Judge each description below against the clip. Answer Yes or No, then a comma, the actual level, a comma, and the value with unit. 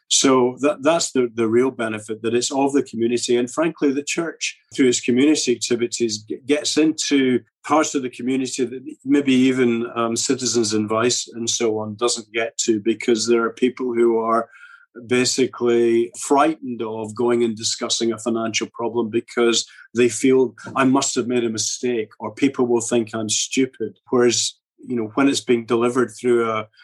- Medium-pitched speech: No, low, 120 Hz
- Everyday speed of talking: Yes, average, 175 wpm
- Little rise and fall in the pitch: Yes, narrow, 2.1 semitones